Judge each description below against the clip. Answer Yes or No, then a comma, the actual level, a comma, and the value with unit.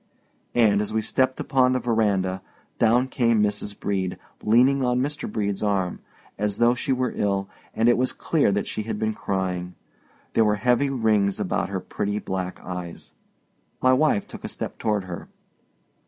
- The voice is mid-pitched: No, low, 105 Hz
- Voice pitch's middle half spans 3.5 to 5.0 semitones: Yes, average, 3.8 semitones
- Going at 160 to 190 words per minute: Yes, average, 170 wpm